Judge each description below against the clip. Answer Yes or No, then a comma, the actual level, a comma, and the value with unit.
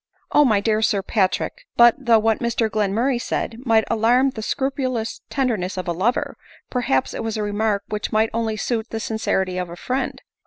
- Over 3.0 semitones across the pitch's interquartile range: No, narrow, 2.5 semitones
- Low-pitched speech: No, high, 220 Hz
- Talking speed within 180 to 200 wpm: Yes, average, 190 wpm